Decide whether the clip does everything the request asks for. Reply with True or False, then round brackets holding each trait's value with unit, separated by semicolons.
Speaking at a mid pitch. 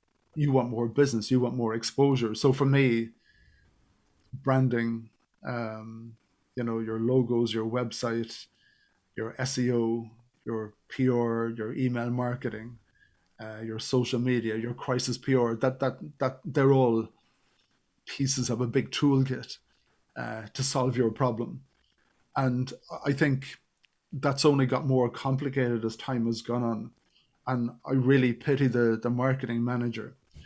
False (125 Hz)